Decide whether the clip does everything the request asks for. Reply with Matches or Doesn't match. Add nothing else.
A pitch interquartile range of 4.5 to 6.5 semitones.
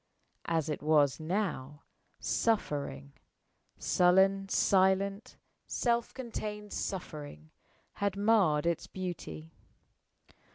Matches